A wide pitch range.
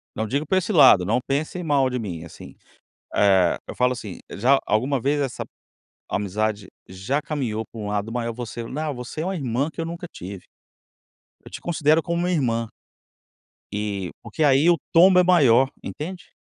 Yes: wide, 6.4 semitones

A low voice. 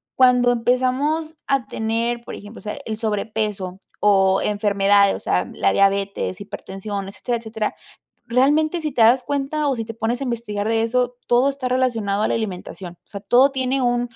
No: high, 230 Hz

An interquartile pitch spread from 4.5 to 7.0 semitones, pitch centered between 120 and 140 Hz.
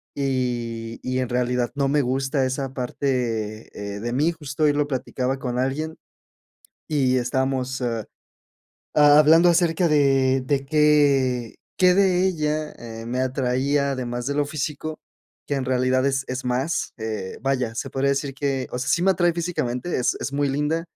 No: average, 2.9 semitones; low, 135 Hz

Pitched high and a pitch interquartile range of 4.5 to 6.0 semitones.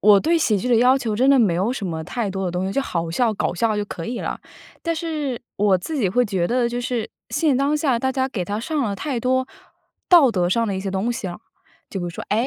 Yes: high, 230 Hz; average, 5.3 semitones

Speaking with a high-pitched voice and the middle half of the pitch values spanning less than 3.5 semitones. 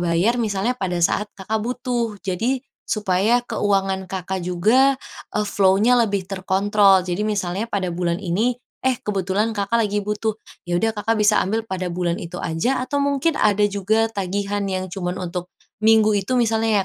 Yes: high, 205 Hz; average, 3.1 semitones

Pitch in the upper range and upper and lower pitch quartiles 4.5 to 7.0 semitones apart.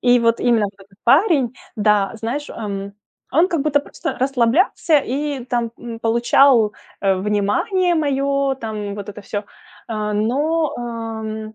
Yes: high, 235 Hz; average, 4.8 semitones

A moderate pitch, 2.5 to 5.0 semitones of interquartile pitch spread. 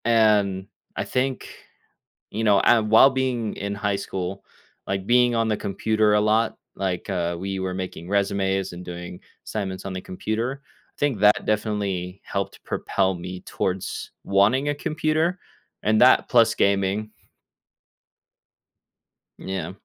No: low, 100 Hz; average, 2.9 semitones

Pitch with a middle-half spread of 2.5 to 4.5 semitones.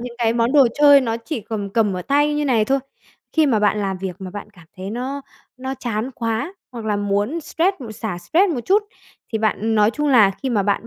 No: average, 5.0 semitones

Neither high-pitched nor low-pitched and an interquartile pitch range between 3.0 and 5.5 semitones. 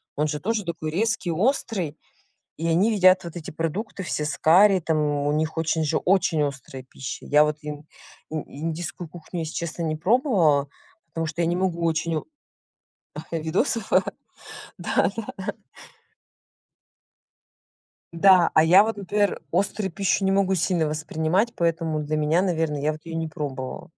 Yes: medium, 165 Hz; average, 3.6 semitones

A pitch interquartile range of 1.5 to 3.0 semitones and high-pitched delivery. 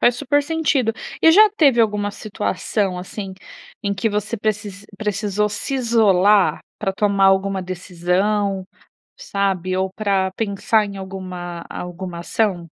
Yes: narrow, 2.4 semitones; high, 200 Hz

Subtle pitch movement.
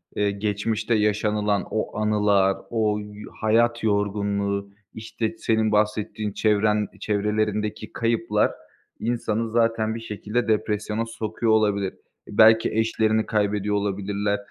Yes: narrow, 1.3 semitones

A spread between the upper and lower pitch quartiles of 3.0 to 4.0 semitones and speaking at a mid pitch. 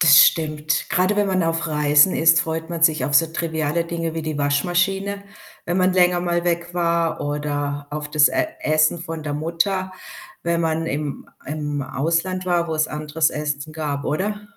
No: narrow, 2.6 semitones; medium, 160 Hz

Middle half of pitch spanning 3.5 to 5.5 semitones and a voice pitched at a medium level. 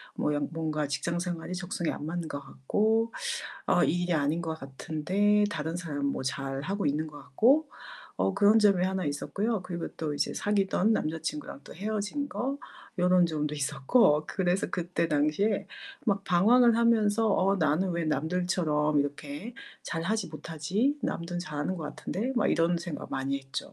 Yes: average, 5.1 semitones; medium, 175 Hz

